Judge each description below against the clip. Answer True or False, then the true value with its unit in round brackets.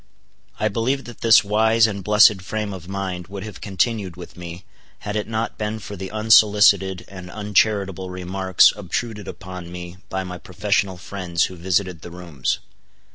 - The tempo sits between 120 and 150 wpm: False (165 wpm)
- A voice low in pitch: True (95 Hz)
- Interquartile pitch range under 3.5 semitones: True (2.8 semitones)